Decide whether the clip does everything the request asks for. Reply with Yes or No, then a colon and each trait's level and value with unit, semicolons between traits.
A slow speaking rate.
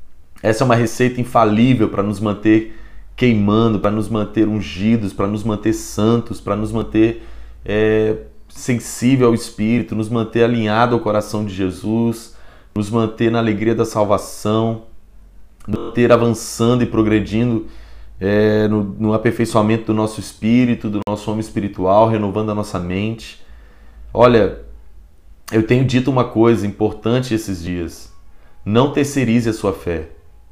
No: average, 140 wpm